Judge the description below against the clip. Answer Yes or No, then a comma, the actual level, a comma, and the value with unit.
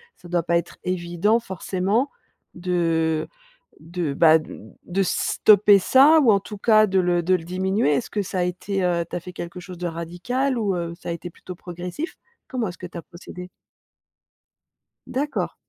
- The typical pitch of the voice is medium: Yes, medium, 180 Hz